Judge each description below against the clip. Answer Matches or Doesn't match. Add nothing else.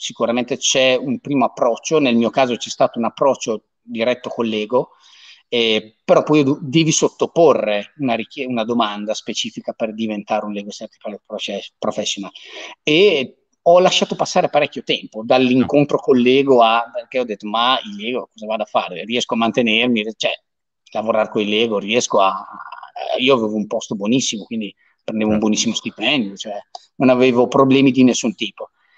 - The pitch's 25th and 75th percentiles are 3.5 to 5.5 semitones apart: Matches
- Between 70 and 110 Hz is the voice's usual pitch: Doesn't match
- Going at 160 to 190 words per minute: Matches